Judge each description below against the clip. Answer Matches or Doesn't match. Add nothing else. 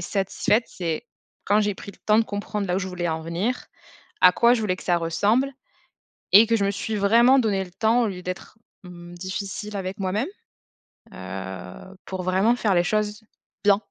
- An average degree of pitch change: Matches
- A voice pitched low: Doesn't match